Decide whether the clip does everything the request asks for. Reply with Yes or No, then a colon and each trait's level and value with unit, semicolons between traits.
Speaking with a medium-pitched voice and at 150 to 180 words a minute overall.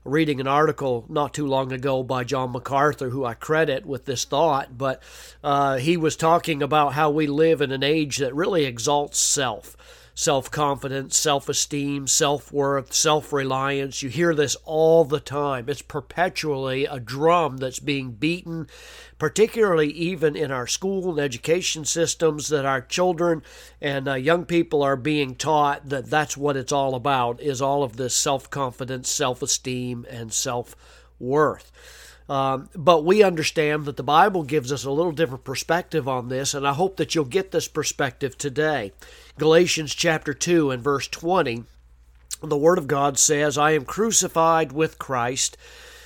Yes: medium, 145 Hz; average, 165 wpm